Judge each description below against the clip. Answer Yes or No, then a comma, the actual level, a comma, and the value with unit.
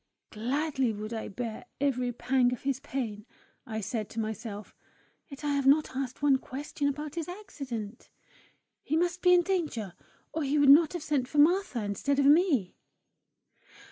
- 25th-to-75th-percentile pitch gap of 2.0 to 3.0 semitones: No, average, 4.6 semitones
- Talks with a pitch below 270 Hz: No, very high, 275 Hz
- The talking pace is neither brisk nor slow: Yes, average, 170 wpm